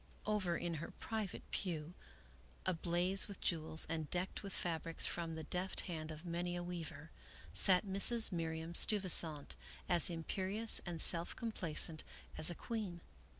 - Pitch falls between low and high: Yes, medium, 175 Hz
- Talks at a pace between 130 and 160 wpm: Yes, average, 145 wpm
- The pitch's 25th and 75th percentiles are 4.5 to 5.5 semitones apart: No, average, 2.7 semitones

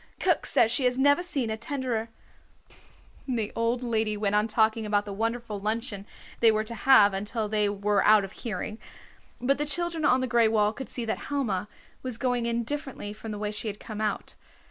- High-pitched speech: Yes, high, 225 Hz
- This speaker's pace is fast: Yes, fast, 210 wpm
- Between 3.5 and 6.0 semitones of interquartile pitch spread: No, average, 3.0 semitones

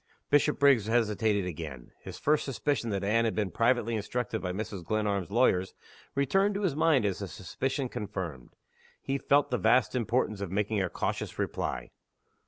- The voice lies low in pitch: Yes, low, 110 Hz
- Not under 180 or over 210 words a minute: No, average, 165 wpm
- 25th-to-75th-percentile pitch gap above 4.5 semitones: Yes, average, 5.1 semitones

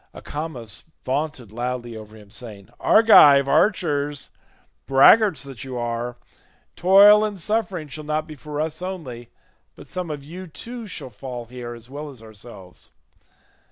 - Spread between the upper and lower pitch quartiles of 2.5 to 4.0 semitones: No, wide, 5.5 semitones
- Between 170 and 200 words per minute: No, average, 145 wpm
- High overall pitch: No, medium, 140 Hz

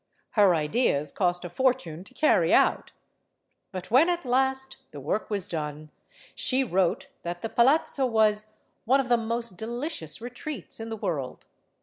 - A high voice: Yes, high, 220 Hz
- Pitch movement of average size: No, wide, 6.5 semitones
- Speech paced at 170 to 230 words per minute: No, average, 155 wpm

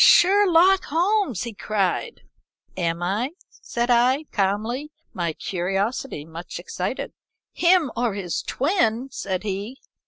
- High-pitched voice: Yes, high, 235 Hz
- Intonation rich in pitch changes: Yes, wide, 8.2 semitones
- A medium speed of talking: No, slow, 115 wpm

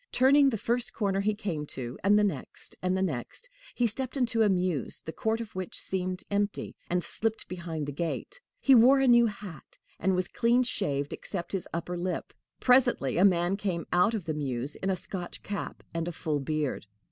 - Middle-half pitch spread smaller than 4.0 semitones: No, average, 4.9 semitones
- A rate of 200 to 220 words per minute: Yes, fast, 205 wpm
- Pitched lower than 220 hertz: Yes, high, 190 Hz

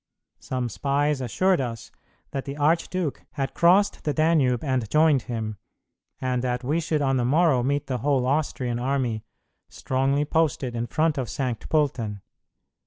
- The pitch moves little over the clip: No, average, 3.6 semitones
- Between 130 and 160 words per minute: Yes, average, 155 wpm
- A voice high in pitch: No, low, 135 Hz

